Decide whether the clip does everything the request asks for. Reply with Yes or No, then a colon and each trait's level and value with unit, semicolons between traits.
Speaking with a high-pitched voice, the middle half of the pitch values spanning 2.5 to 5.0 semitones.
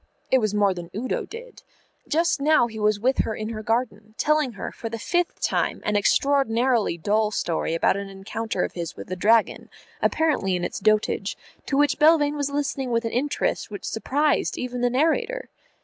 No: high, 230 Hz; wide, 5.4 semitones